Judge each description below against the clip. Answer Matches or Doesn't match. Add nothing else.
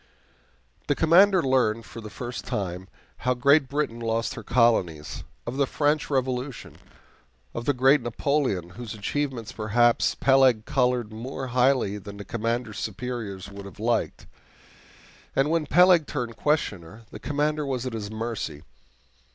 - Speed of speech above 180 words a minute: Doesn't match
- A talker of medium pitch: Doesn't match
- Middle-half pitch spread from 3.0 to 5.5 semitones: Matches